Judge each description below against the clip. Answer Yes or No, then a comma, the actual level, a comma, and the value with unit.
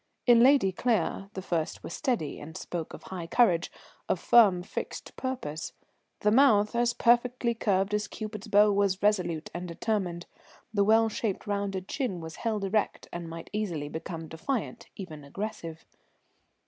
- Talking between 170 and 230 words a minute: No, average, 155 wpm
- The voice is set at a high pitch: Yes, high, 200 Hz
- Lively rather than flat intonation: No, average, 4.6 semitones